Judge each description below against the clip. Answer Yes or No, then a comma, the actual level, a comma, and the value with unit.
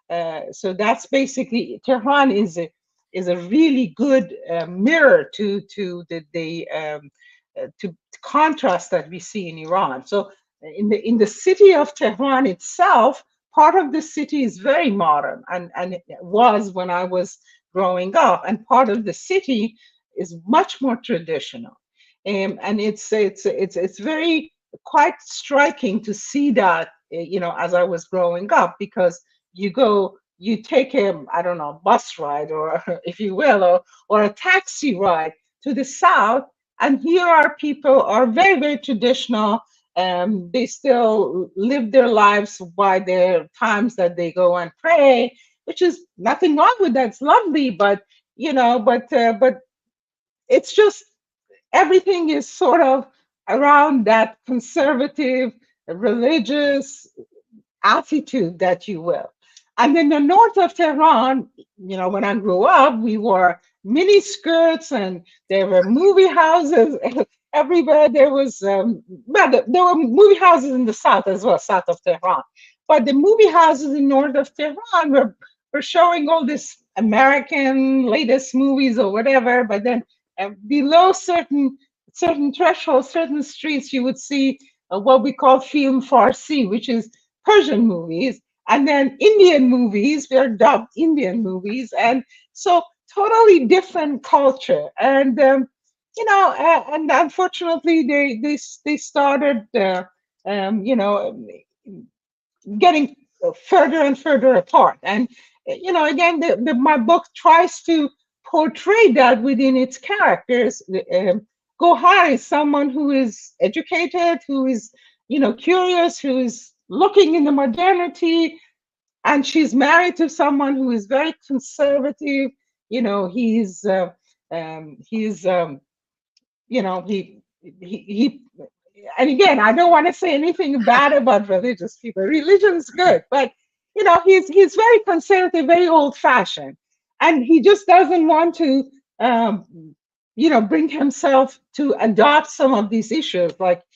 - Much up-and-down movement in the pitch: Yes, wide, 7.5 semitones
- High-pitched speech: Yes, very high, 270 Hz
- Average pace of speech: Yes, average, 150 wpm